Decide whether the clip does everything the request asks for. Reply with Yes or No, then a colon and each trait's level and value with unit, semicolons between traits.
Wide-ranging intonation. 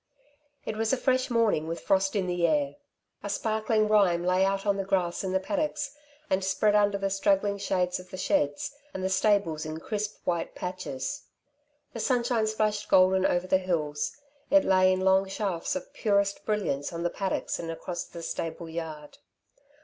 No: average, 3.4 semitones